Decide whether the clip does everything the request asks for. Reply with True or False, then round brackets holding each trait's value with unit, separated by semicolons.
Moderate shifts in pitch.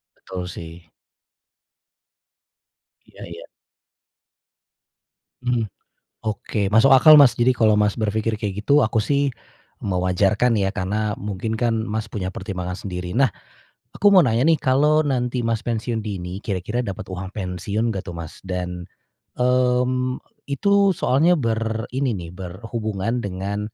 True (4.7 semitones)